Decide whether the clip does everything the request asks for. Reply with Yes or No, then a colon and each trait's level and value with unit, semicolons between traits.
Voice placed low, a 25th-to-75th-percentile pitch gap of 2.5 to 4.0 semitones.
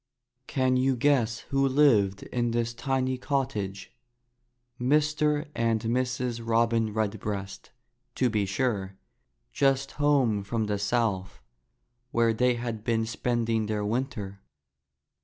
Yes: low, 115 Hz; average, 3.3 semitones